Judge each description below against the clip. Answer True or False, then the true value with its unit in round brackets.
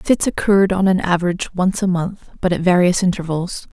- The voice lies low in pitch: False (185 Hz)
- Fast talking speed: True (210 wpm)